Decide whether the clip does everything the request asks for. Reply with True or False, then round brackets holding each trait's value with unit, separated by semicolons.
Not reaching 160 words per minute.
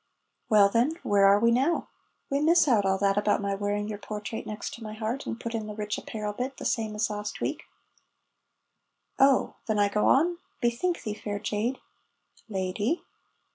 False (185 wpm)